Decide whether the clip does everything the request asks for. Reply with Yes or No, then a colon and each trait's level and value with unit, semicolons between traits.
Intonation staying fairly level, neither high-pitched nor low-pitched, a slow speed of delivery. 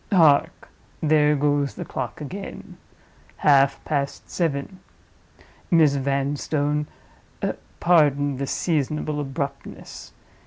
Yes: narrow, 1.7 semitones; medium, 145 Hz; slow, 80 wpm